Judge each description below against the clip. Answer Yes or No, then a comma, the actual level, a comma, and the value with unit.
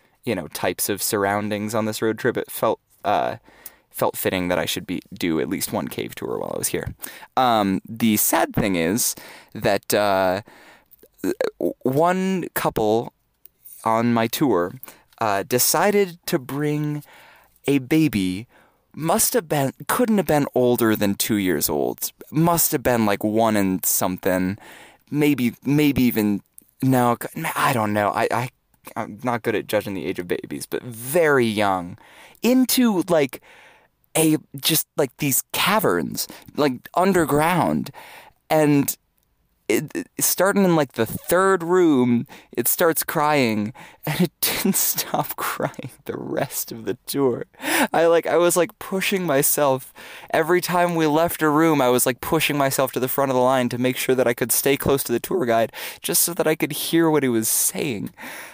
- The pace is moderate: Yes, average, 165 wpm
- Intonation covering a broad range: Yes, wide, 6.4 semitones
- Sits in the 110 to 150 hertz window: Yes, medium, 140 Hz